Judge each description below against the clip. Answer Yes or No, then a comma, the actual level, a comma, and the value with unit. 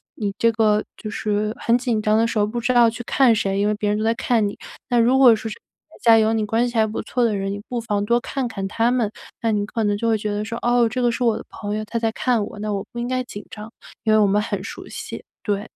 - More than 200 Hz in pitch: Yes, high, 220 Hz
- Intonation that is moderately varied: No, narrow, 2.1 semitones